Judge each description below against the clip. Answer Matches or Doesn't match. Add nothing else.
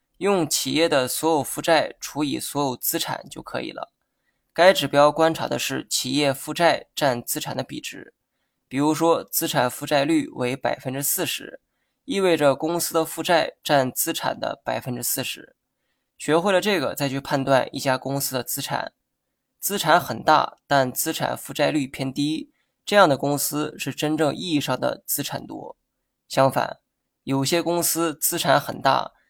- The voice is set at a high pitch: Doesn't match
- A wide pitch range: Doesn't match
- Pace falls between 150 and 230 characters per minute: Doesn't match